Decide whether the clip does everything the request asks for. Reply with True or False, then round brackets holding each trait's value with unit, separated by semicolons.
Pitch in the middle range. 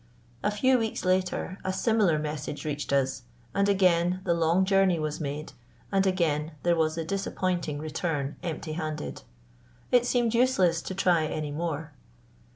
True (170 Hz)